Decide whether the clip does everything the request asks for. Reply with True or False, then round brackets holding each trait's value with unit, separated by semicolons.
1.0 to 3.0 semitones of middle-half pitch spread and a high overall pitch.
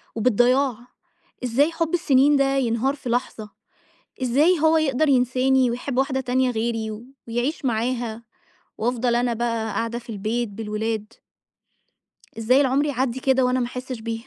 True (2.6 semitones; 250 Hz)